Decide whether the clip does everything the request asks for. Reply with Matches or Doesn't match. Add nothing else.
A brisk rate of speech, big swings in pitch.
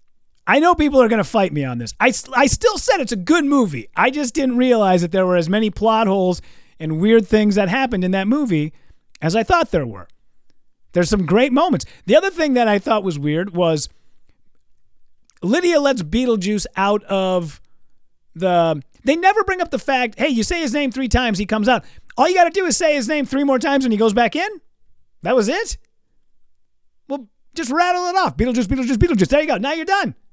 Matches